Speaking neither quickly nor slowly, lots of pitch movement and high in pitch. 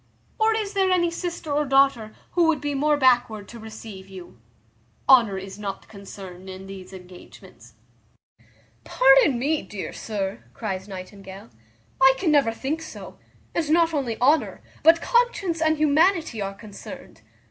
Yes: average, 145 wpm; wide, 8.2 semitones; very high, 250 Hz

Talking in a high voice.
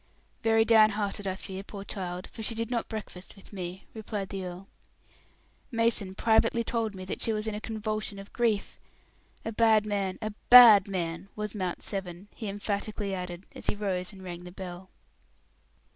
Yes: high, 205 Hz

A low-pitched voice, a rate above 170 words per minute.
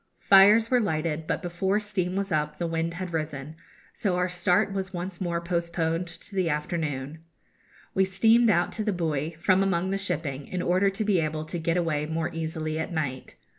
No: medium, 175 Hz; average, 195 wpm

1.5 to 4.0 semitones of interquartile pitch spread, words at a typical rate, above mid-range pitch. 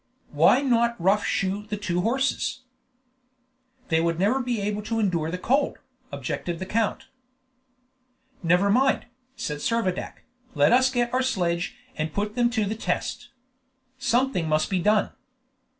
No: average, 5.3 semitones; average, 145 wpm; high, 210 Hz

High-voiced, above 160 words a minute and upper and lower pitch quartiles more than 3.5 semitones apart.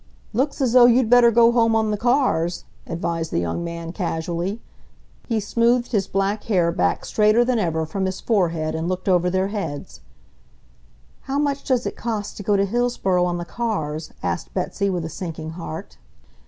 Yes: high, 195 Hz; average, 180 wpm; wide, 5.6 semitones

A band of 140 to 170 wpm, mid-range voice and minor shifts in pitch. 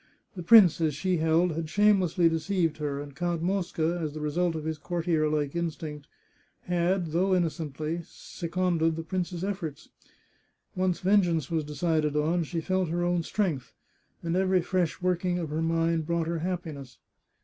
Yes: average, 160 wpm; medium, 170 Hz; narrow, 2.3 semitones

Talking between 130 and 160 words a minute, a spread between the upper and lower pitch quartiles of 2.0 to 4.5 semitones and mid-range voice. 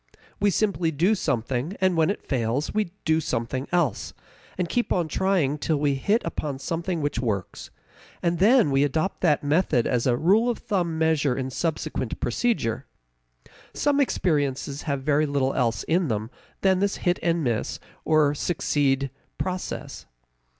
No: average, 155 wpm; average, 5.1 semitones; medium, 155 Hz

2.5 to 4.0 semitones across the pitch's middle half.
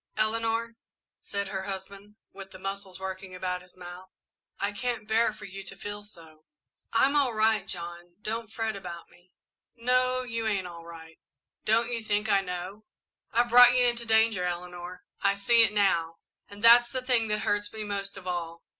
Yes: average, 3.7 semitones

